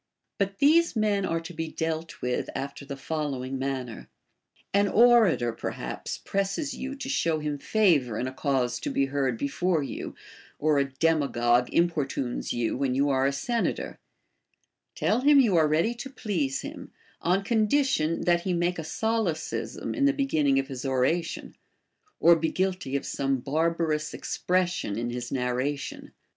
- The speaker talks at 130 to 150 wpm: No, average, 160 wpm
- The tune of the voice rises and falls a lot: Yes, wide, 6.4 semitones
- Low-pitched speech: No, medium, 155 Hz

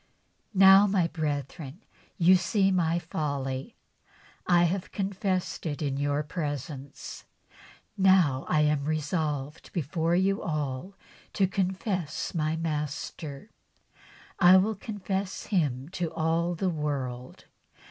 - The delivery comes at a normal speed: No, slow, 115 wpm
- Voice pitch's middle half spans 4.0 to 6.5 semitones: Yes, average, 4.5 semitones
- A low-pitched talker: No, medium, 165 Hz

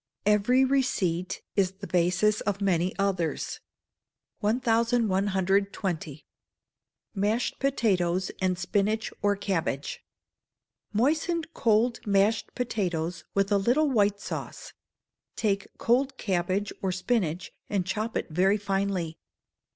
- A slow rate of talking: Yes, slow, 105 wpm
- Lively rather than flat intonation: No, average, 3.2 semitones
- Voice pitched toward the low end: No, high, 200 Hz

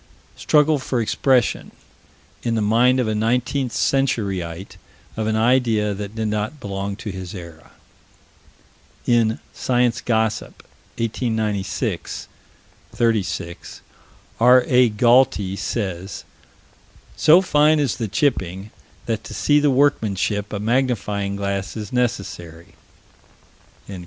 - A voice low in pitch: Yes, low, 110 Hz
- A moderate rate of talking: No, slow, 110 wpm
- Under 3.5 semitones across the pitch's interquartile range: No, average, 4.0 semitones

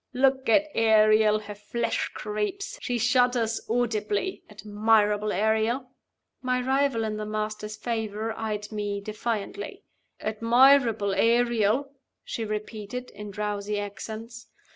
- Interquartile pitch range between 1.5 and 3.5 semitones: Yes, narrow, 2.4 semitones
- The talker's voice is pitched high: Yes, high, 220 Hz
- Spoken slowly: Yes, slow, 110 wpm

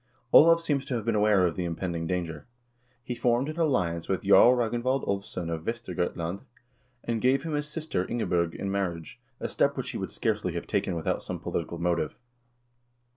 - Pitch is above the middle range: No, low, 100 Hz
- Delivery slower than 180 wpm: No, average, 190 wpm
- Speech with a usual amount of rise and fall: No, wide, 6.6 semitones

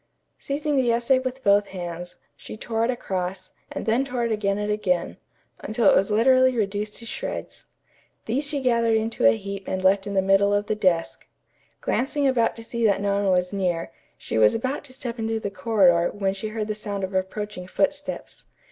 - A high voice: Yes, high, 210 Hz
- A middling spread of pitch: Yes, average, 3.4 semitones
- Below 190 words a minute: No, average, 200 wpm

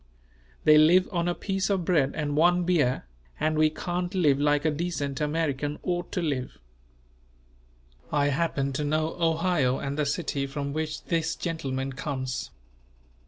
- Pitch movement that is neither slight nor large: Yes, average, 3.3 semitones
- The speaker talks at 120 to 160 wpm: Yes, average, 155 wpm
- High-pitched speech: No, medium, 155 Hz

